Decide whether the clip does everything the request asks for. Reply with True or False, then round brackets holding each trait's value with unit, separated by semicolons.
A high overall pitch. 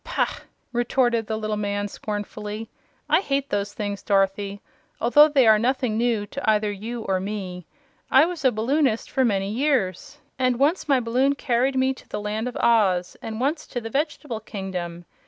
True (225 Hz)